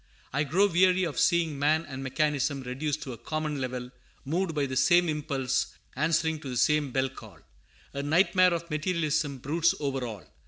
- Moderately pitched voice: Yes, medium, 150 Hz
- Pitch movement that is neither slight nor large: Yes, average, 3.6 semitones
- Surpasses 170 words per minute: Yes, average, 180 wpm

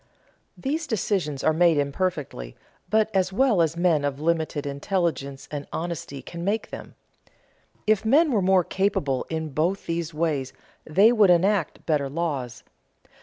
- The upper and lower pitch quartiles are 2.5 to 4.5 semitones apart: No, average, 4.9 semitones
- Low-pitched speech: No, medium, 170 Hz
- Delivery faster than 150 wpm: No, average, 145 wpm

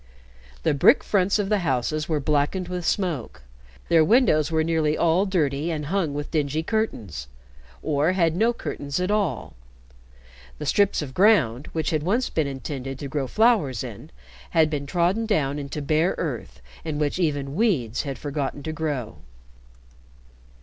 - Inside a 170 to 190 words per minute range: No, average, 160 wpm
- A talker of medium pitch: Yes, medium, 155 Hz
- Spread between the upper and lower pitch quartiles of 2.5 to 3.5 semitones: No, average, 4.3 semitones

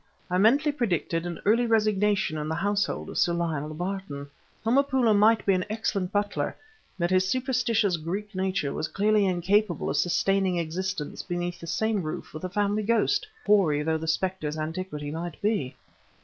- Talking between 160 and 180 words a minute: Yes, average, 165 wpm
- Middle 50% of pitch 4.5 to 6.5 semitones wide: No, average, 4.0 semitones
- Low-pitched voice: No, high, 190 Hz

